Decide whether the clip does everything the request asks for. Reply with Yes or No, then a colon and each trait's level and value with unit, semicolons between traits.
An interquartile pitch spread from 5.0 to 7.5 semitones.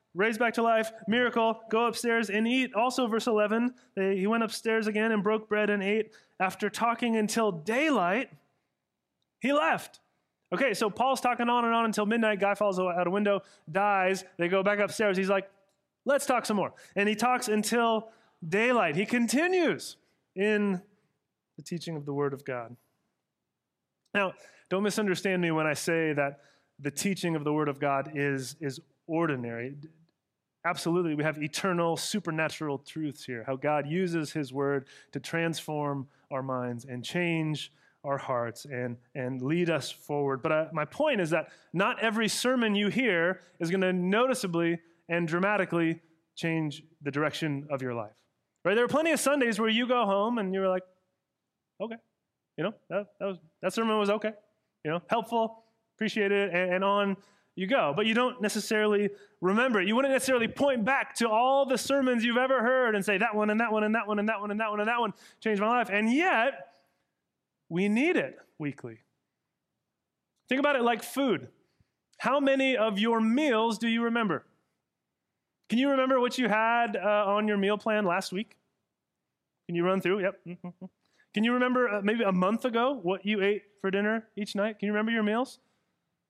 Yes: wide, 5.4 semitones